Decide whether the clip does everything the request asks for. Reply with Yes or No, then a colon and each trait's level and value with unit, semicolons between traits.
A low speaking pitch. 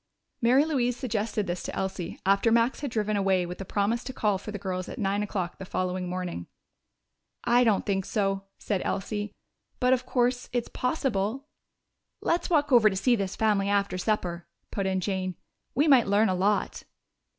No: high, 205 Hz